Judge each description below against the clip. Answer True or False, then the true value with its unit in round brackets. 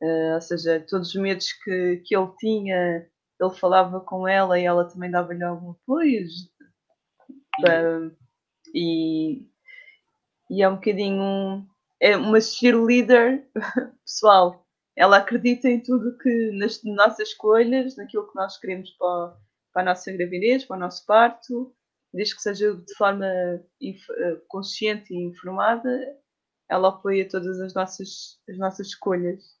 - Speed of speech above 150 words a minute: False (140 wpm)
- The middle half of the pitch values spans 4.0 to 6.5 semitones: True (4.6 semitones)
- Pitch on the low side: False (195 Hz)